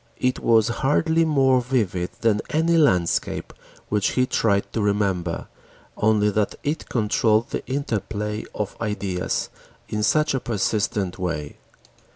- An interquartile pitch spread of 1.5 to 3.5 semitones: No, average, 4.3 semitones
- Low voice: Yes, low, 110 Hz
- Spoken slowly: Yes, slow, 130 wpm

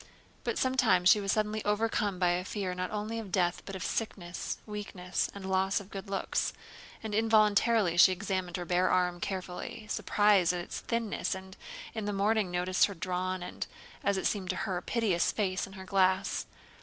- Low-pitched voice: No, high, 190 Hz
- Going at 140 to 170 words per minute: No, average, 180 wpm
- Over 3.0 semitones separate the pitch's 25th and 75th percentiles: No, narrow, 2.4 semitones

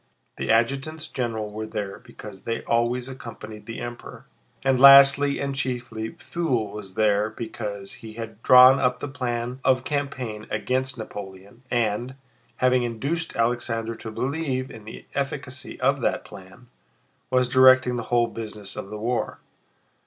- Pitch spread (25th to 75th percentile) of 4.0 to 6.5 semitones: No, average, 3.0 semitones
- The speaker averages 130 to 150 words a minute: Yes, average, 145 wpm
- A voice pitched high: No, low, 120 Hz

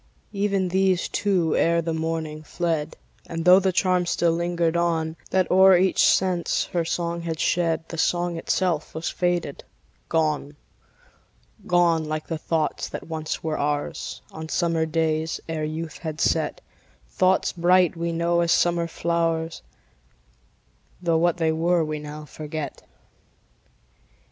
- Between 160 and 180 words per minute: No, average, 140 wpm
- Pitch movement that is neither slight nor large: No, narrow, 1.6 semitones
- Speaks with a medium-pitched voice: Yes, medium, 165 Hz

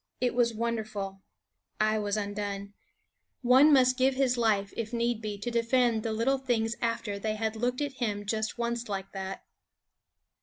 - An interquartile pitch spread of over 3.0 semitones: No, average, 2.7 semitones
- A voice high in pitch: Yes, high, 225 Hz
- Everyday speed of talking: Yes, average, 165 wpm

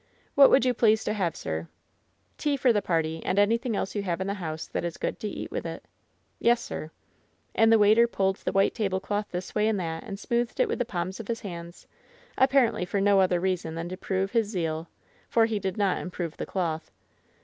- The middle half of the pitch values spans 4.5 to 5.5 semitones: No, average, 4.1 semitones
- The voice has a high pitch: Yes, high, 195 Hz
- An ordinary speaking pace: No, fast, 225 wpm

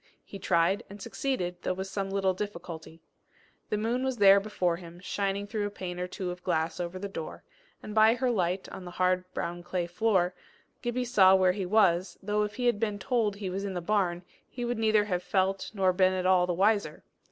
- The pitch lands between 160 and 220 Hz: Yes, high, 190 Hz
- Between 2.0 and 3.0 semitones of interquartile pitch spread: Yes, average, 2.7 semitones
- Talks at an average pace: No, fast, 220 wpm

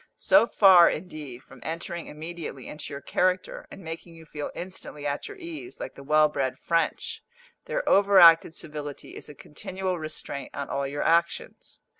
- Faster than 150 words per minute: Yes, average, 170 wpm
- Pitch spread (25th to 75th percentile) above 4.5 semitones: No, average, 3.9 semitones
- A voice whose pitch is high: No, medium, 165 Hz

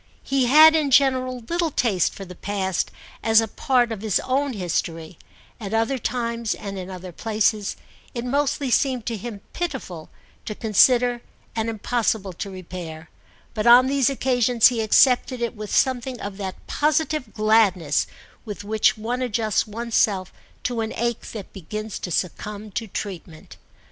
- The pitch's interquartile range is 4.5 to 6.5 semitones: No, average, 3.9 semitones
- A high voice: Yes, high, 225 Hz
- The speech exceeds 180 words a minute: No, average, 160 wpm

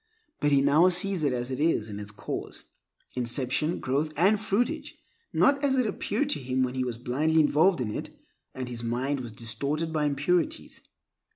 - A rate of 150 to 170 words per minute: No, average, 185 wpm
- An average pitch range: No, wide, 5.7 semitones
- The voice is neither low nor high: Yes, medium, 145 Hz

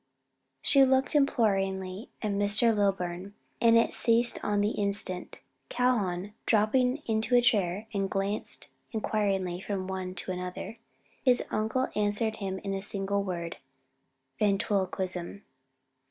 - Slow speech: Yes, slow, 125 wpm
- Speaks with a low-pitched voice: No, high, 205 Hz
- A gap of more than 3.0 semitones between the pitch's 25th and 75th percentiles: No, average, 2.7 semitones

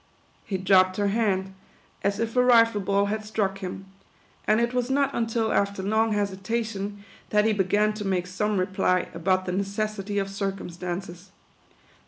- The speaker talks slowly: No, average, 165 wpm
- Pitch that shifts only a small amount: Yes, narrow, 2.3 semitones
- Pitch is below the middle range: No, high, 200 Hz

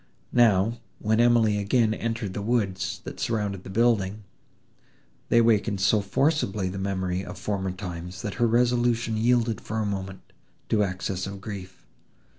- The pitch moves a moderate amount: Yes, average, 3.3 semitones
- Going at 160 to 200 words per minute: No, average, 150 wpm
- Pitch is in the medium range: No, low, 105 Hz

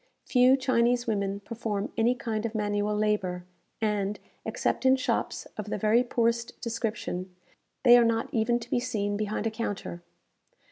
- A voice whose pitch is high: Yes, high, 220 Hz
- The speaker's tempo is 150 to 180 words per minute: Yes, average, 155 wpm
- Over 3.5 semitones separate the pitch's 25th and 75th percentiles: No, narrow, 2.5 semitones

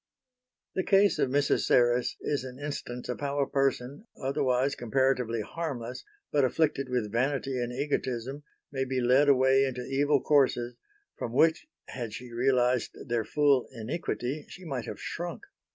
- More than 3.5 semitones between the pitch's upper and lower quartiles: No, narrow, 2.6 semitones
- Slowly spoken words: No, average, 150 wpm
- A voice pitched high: No, low, 130 Hz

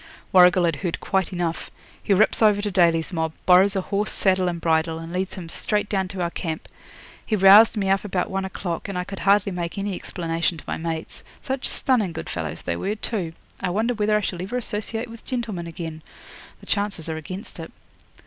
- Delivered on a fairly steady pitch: No, average, 3.5 semitones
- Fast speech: Yes, fast, 210 wpm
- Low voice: No, medium, 185 Hz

